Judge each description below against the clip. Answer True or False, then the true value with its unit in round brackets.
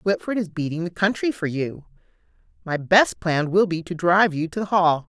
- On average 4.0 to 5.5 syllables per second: True (5.2 syllables/s)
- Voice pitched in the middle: True (180 Hz)